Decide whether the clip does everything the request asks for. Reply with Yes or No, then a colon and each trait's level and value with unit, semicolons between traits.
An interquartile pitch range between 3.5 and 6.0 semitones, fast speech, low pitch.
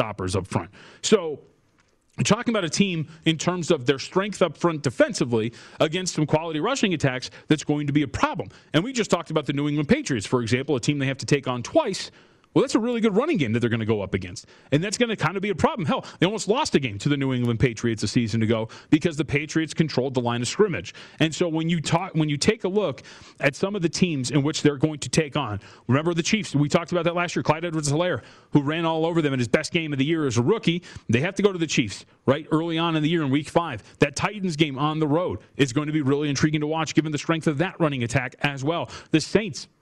No: average, 4.1 semitones; fast, 270 wpm; medium, 155 Hz